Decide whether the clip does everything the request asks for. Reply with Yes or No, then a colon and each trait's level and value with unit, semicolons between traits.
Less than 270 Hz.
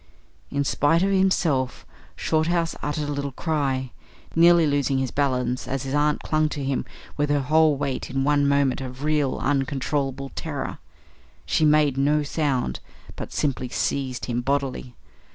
Yes: medium, 140 Hz